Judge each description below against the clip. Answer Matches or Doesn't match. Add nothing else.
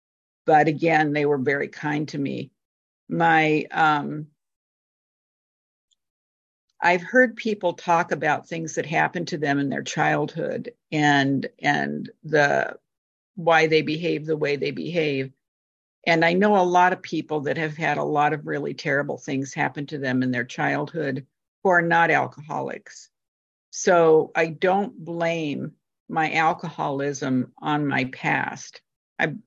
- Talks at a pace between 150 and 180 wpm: Doesn't match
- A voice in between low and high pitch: Matches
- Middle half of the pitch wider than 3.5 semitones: Doesn't match